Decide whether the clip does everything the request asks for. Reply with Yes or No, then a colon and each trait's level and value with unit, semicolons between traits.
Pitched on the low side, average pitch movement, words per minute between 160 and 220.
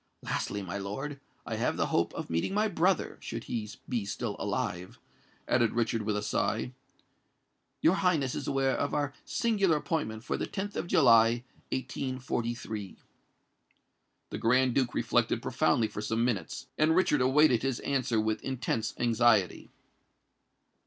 No: low, 120 Hz; average, 4.5 semitones; average, 145 wpm